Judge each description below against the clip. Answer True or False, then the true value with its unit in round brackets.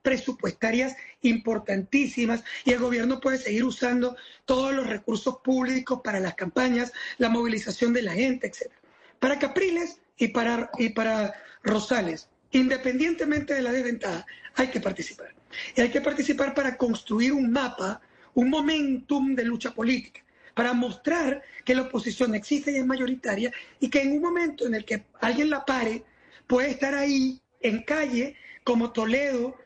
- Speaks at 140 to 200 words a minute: True (150 wpm)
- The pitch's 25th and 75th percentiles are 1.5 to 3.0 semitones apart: True (2.5 semitones)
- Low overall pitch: False (255 Hz)